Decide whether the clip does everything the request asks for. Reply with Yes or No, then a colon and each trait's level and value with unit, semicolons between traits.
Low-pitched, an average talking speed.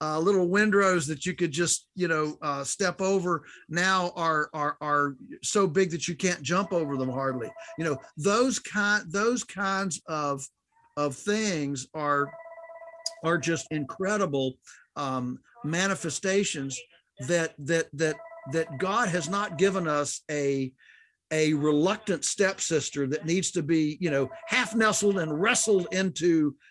No: medium, 170 Hz; average, 145 wpm